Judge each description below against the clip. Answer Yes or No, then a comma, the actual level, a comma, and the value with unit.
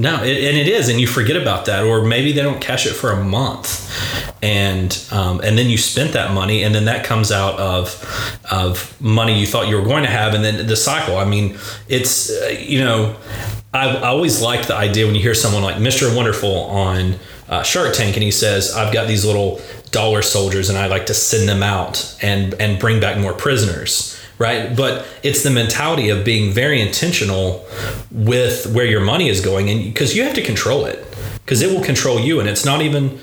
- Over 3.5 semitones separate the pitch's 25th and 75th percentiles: Yes, average, 4.1 semitones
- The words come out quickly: Yes, fast, 220 wpm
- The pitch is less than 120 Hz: Yes, low, 110 Hz